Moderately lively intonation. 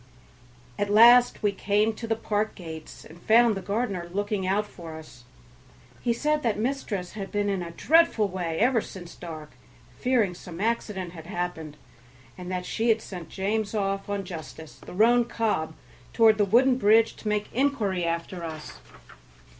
Yes: average, 4.1 semitones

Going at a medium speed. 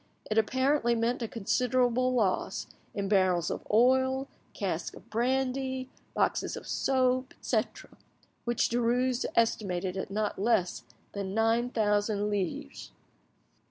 No: slow, 120 wpm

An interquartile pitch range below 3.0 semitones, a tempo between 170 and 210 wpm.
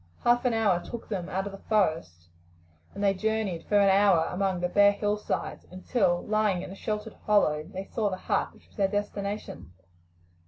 Yes: narrow, 2.4 semitones; average, 190 wpm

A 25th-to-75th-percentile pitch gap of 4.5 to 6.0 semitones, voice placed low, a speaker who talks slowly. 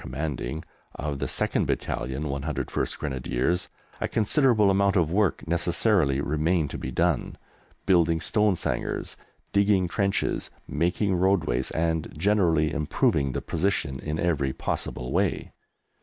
Yes: average, 5.0 semitones; very low, 85 Hz; slow, 115 wpm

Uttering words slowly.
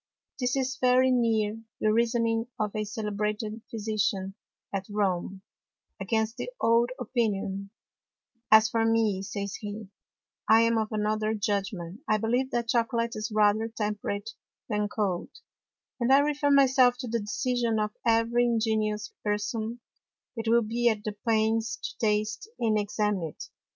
No: average, 145 wpm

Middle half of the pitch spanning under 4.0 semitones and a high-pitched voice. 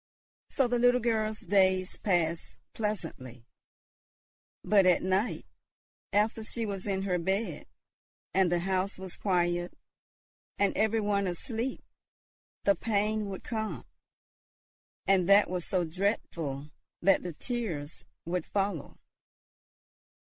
Yes: average, 3.4 semitones; high, 195 Hz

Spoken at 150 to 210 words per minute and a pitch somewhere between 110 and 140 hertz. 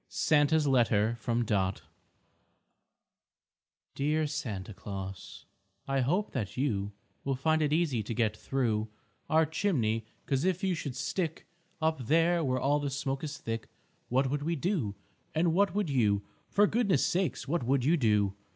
Yes: average, 155 wpm; low, 135 Hz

